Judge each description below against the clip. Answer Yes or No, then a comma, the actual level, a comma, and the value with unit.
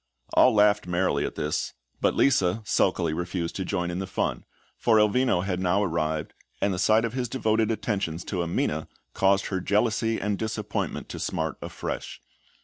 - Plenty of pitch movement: No, average, 3.8 semitones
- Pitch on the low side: Yes, very low, 95 Hz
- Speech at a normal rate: Yes, average, 170 wpm